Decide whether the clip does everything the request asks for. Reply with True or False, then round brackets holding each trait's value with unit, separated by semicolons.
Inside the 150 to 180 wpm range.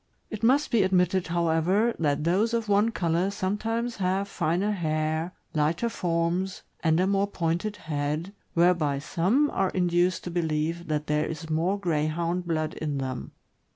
True (155 wpm)